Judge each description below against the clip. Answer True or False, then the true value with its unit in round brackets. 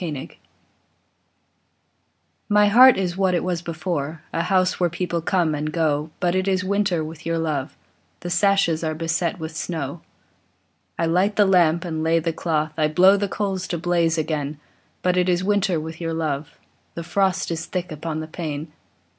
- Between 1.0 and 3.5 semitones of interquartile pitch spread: True (2.6 semitones)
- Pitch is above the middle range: False (170 Hz)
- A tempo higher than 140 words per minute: True (180 wpm)